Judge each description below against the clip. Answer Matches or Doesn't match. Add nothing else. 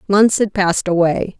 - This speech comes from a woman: Matches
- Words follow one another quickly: Doesn't match